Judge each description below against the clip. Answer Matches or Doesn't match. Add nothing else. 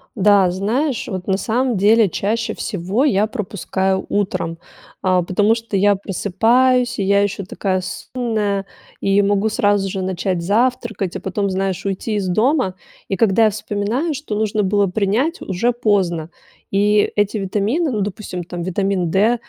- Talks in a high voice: Matches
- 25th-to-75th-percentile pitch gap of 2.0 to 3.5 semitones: Matches